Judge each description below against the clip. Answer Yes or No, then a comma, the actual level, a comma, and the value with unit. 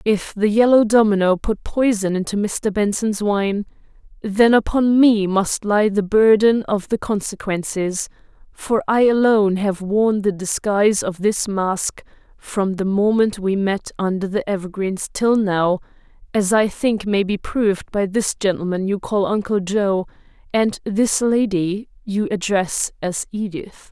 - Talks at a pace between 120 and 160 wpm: Yes, average, 150 wpm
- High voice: Yes, high, 205 Hz